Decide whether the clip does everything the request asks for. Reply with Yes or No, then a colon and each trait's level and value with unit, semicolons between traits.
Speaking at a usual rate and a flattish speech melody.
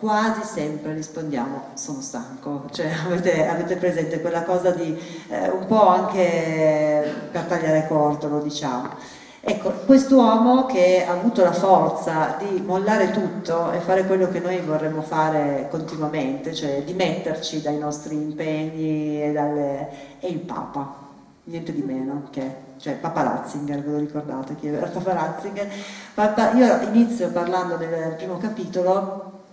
No: average, 140 wpm; average, 3.6 semitones